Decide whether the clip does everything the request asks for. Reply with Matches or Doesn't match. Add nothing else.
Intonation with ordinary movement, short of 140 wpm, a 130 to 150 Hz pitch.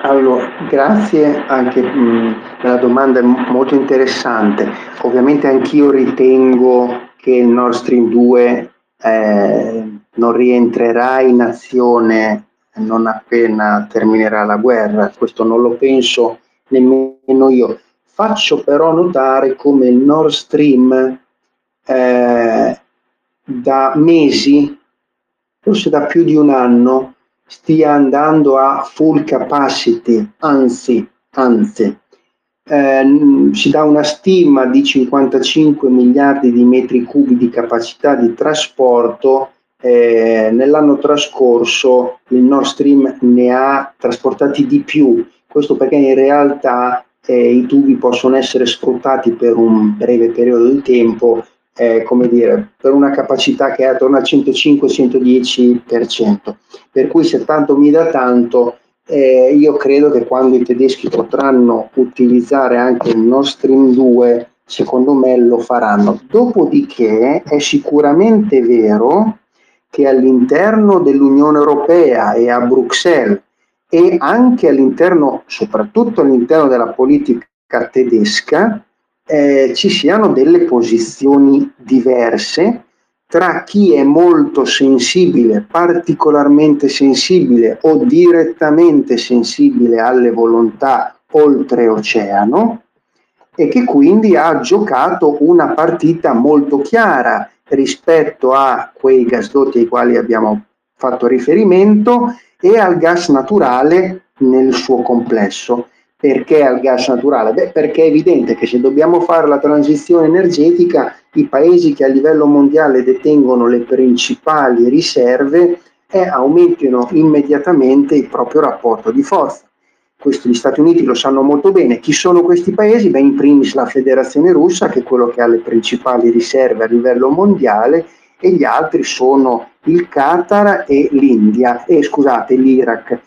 Matches